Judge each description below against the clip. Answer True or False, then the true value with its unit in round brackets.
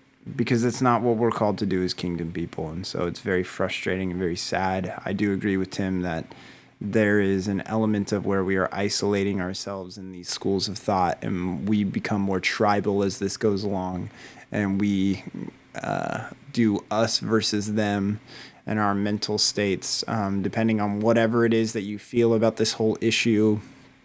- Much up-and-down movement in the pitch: False (2.4 semitones)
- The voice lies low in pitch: True (100 Hz)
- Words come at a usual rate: True (180 wpm)